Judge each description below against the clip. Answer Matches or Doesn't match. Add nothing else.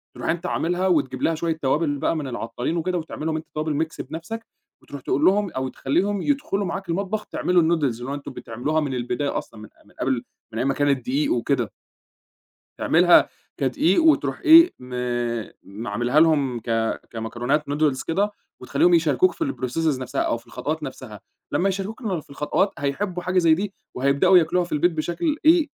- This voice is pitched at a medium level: Matches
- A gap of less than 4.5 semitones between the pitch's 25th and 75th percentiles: Doesn't match